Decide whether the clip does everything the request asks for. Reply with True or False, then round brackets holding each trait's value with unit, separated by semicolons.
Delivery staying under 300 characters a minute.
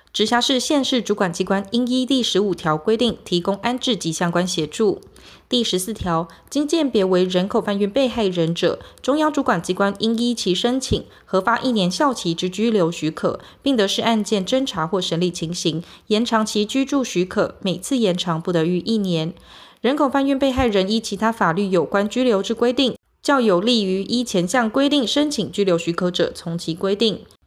True (285 characters per minute)